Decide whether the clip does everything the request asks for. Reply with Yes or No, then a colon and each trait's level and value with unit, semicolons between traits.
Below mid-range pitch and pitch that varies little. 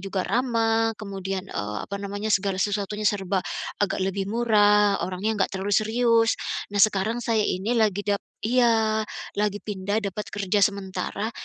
No: high, 205 Hz; narrow, 2.0 semitones